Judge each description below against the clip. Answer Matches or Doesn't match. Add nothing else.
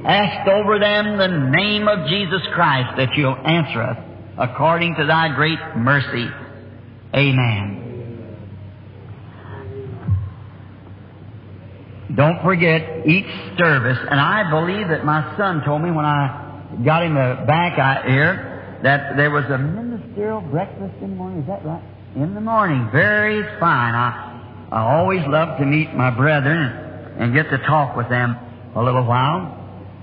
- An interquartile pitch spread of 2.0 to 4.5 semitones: Doesn't match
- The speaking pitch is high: Doesn't match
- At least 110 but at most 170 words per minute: Matches